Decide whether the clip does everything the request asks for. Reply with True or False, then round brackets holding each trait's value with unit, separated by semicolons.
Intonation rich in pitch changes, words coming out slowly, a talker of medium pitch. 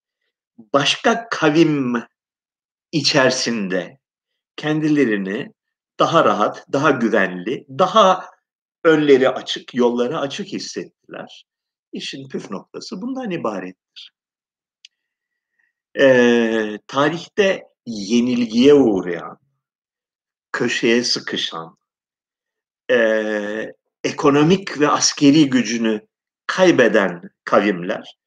True (9.0 semitones; 70 wpm; 145 Hz)